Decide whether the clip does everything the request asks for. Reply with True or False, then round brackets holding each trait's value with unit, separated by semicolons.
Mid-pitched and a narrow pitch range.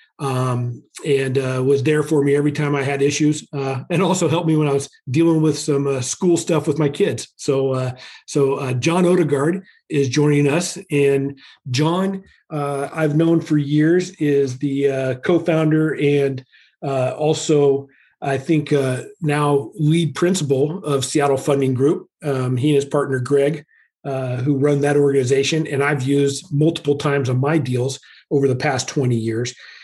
True (145 Hz; 2.2 semitones)